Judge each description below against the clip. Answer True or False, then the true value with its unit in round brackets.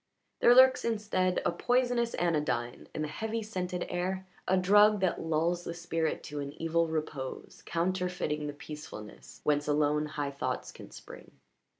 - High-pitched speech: False (170 Hz)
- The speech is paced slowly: False (155 wpm)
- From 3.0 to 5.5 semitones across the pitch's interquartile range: True (3.9 semitones)